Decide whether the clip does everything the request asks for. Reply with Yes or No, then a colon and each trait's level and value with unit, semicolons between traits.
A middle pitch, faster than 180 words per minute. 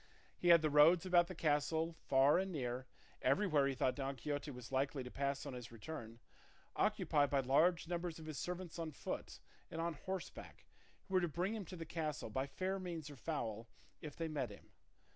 Yes: medium, 155 Hz; average, 200 wpm